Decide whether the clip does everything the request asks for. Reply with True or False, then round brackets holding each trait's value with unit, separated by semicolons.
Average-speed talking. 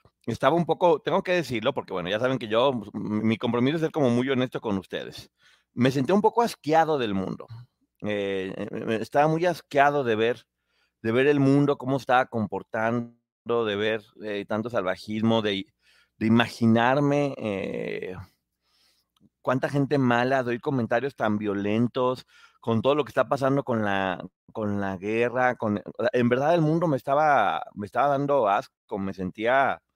True (160 wpm)